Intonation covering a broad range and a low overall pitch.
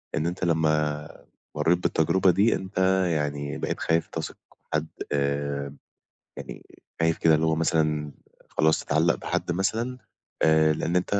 No: narrow, 2.4 semitones; very low, 80 Hz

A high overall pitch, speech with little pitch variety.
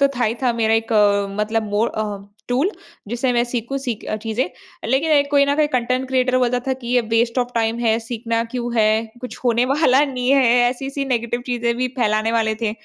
Yes: high, 240 Hz; narrow, 2.3 semitones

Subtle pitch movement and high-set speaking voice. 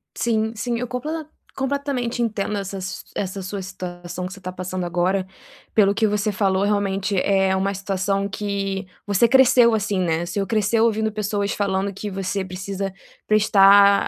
Yes: narrow, 2.2 semitones; high, 200 Hz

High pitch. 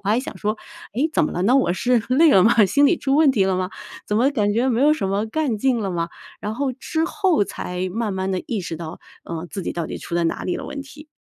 Yes: high, 220 Hz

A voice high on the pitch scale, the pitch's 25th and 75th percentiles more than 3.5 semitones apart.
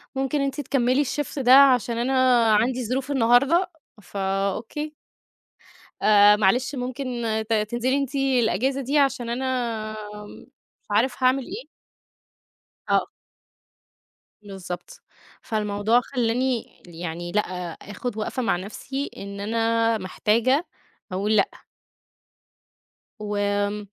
Yes: high, 235 Hz; average, 4.3 semitones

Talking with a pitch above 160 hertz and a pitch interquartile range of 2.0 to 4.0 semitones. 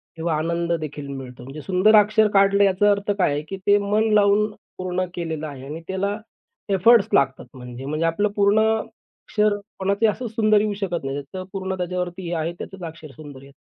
No: medium, 185 Hz; average, 4.7 semitones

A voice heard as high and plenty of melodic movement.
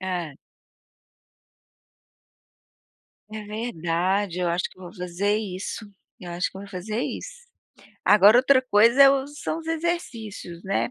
Yes: high, 205 Hz; wide, 5.8 semitones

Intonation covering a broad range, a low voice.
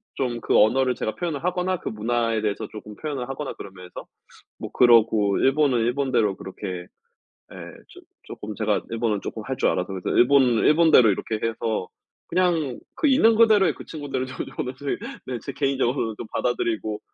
No: average, 4.6 semitones; low, 120 Hz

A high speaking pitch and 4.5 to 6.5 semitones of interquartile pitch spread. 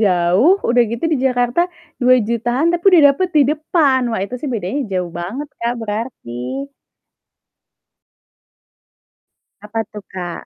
Yes: high, 240 Hz; average, 5.3 semitones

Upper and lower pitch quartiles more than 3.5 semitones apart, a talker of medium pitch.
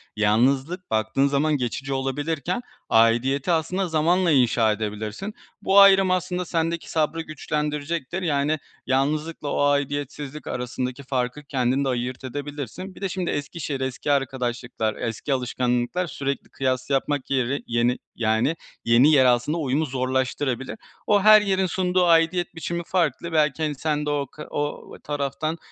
Yes: average, 4.2 semitones; medium, 145 Hz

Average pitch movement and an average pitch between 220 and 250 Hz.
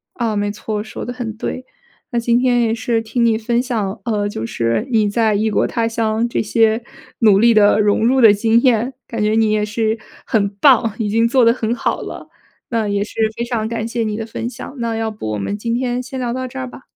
No: narrow, 1.9 semitones; high, 225 Hz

